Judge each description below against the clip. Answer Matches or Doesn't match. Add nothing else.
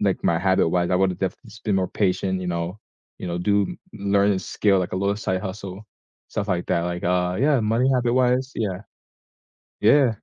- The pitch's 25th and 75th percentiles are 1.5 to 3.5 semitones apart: Matches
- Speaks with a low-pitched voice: Matches